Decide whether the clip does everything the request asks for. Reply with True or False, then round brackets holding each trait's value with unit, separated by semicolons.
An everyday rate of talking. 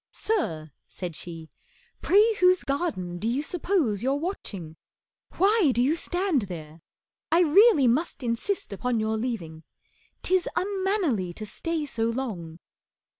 False (130 wpm)